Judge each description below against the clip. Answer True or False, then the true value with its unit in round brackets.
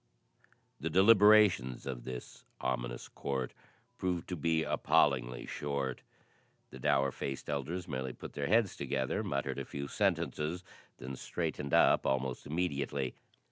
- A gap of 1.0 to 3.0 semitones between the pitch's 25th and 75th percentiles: False (4.3 semitones)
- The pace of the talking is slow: True (130 wpm)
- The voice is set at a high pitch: False (70 Hz)